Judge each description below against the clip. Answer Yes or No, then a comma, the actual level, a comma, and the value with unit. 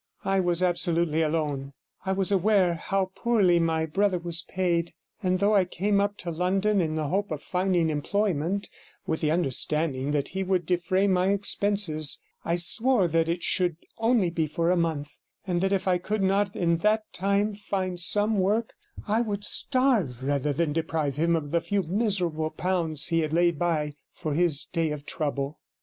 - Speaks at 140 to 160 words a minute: No, average, 180 wpm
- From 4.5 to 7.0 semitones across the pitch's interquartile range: No, average, 3.6 semitones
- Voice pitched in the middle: Yes, medium, 175 Hz